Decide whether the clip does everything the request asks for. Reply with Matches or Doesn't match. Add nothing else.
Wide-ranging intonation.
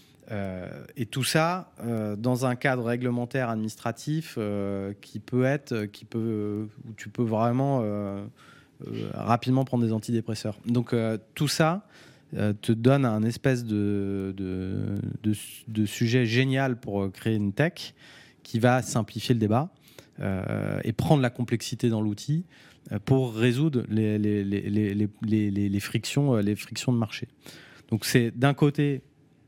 Doesn't match